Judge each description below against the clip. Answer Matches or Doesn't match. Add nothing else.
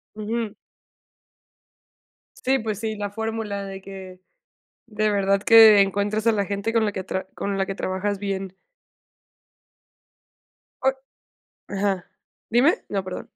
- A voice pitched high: Matches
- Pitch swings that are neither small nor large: Doesn't match